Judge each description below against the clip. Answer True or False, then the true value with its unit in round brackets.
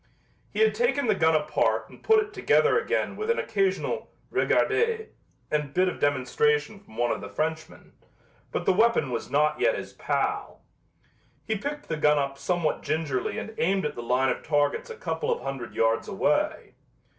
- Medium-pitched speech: True (180 Hz)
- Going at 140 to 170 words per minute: False (180 wpm)